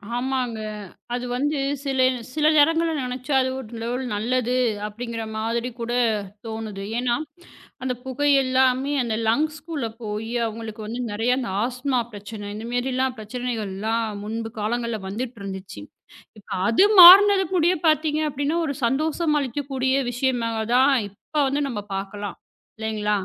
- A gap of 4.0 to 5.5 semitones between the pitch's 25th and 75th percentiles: No, average, 3.5 semitones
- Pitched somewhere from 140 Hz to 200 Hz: No, high, 245 Hz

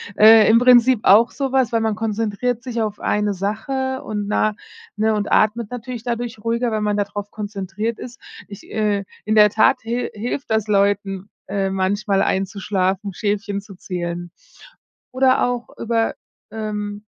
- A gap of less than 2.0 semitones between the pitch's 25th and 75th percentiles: No, narrow, 2.4 semitones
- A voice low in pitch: No, high, 215 Hz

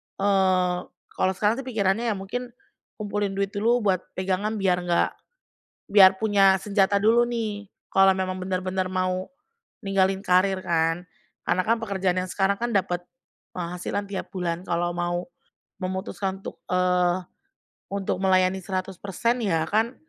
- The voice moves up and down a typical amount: No, narrow, 1.9 semitones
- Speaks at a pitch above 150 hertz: Yes, high, 190 Hz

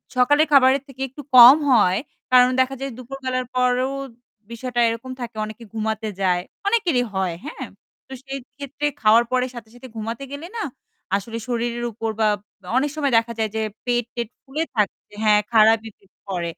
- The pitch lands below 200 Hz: No, high, 240 Hz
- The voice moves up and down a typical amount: Yes, average, 3.2 semitones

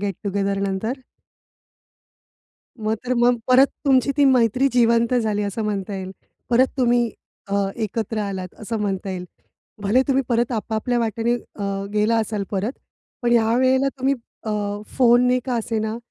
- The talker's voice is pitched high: Yes, high, 225 Hz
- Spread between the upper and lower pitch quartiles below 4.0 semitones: Yes, average, 3.3 semitones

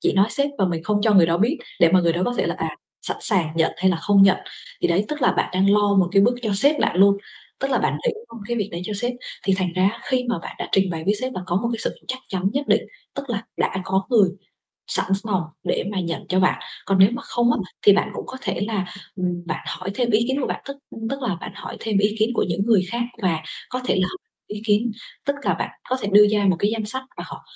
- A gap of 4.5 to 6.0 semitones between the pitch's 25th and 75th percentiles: No, average, 4.1 semitones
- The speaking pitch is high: Yes, high, 205 Hz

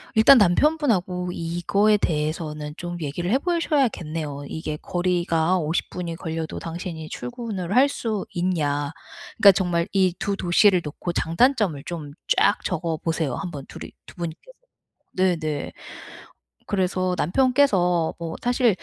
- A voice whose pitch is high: No, medium, 175 Hz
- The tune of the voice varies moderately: Yes, average, 3.9 semitones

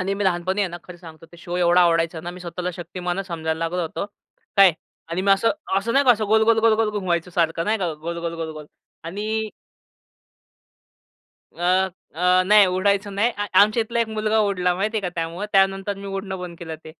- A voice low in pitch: No, medium, 185 Hz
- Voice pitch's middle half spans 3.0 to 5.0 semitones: Yes, average, 3.3 semitones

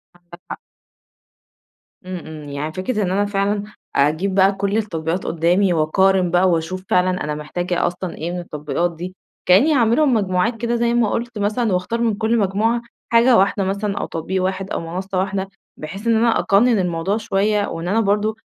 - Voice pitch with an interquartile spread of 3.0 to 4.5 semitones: Yes, average, 3.5 semitones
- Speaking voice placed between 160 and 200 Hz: Yes, high, 190 Hz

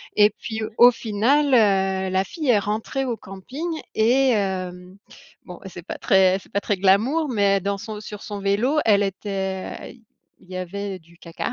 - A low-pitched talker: No, high, 200 Hz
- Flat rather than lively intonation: No, average, 3.4 semitones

